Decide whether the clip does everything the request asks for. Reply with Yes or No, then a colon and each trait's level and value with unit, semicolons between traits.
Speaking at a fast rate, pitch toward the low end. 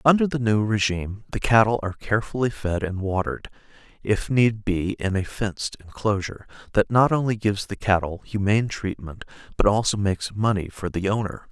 No: average, 170 wpm; low, 105 Hz